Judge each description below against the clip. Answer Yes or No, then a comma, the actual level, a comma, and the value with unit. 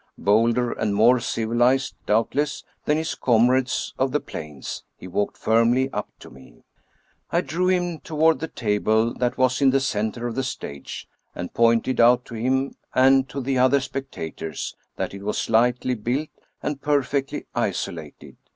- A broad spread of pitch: No, average, 3.3 semitones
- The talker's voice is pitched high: No, low, 125 Hz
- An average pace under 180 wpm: Yes, average, 160 wpm